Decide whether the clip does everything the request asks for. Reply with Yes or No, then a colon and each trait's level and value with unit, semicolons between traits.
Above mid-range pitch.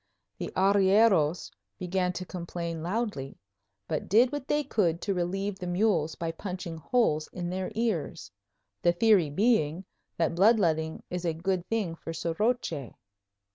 No: medium, 180 Hz